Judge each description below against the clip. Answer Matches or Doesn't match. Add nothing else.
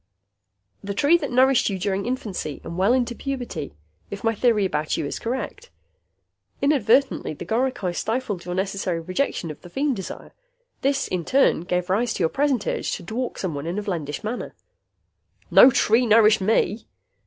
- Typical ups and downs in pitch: Doesn't match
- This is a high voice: Matches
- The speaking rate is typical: Matches